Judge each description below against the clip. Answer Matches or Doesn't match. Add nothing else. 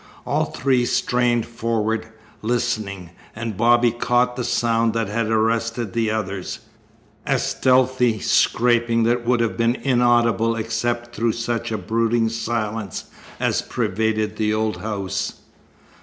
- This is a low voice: Matches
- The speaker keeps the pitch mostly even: Matches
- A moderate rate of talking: Doesn't match